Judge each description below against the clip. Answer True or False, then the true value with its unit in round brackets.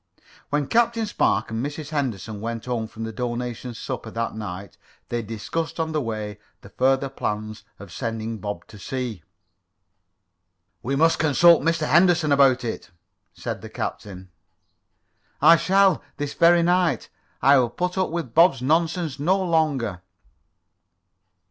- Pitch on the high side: False (130 Hz)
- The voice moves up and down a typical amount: False (6.5 semitones)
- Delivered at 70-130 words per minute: False (140 wpm)